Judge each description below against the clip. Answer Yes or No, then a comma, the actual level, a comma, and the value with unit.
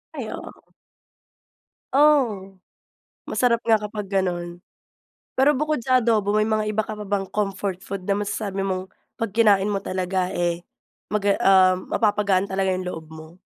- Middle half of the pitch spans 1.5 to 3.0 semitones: Yes, narrow, 2.5 semitones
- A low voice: No, high, 200 Hz